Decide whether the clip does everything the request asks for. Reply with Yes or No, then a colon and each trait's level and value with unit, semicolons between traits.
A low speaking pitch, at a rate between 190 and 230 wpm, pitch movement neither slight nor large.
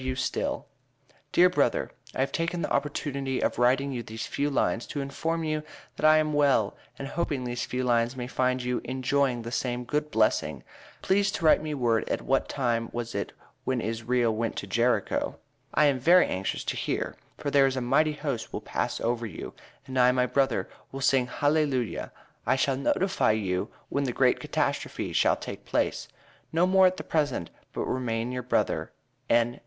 Yes: low, 130 Hz; average, 195 wpm; average, 3.3 semitones